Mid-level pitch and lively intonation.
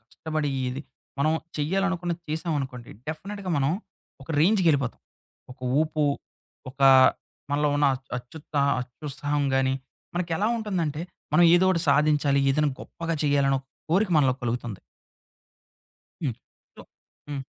No: medium, 150 Hz; average, 3.5 semitones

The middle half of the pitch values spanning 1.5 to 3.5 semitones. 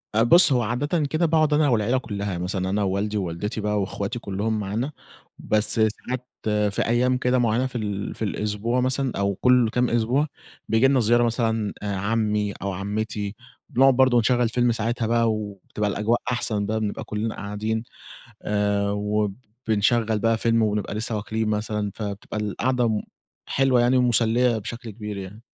Yes: average, 2.8 semitones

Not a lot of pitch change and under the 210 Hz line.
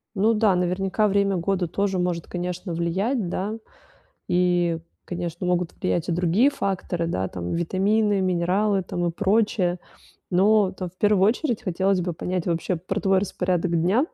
Yes: narrow, 2.3 semitones; medium, 185 Hz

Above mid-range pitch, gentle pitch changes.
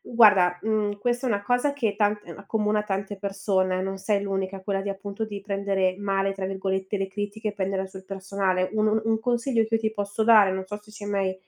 Yes: high, 200 Hz; narrow, 1.8 semitones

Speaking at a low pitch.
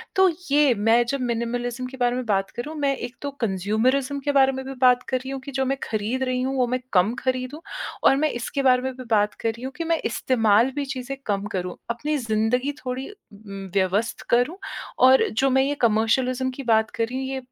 No: very high, 255 Hz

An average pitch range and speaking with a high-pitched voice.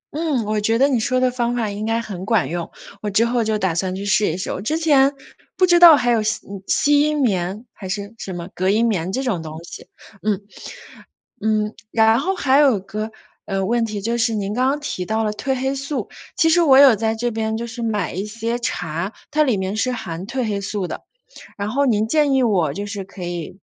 Yes: average, 4.3 semitones; high, 220 Hz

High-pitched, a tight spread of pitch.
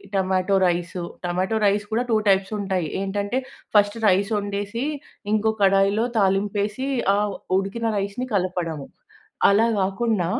Yes: high, 200 Hz; narrow, 1.6 semitones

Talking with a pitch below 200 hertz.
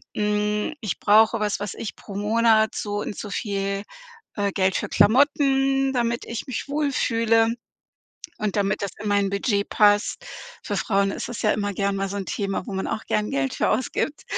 No: high, 210 Hz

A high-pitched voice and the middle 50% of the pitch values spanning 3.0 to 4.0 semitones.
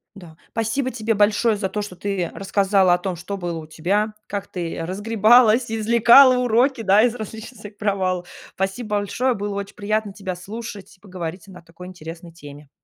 Yes: high, 200 Hz; average, 3.4 semitones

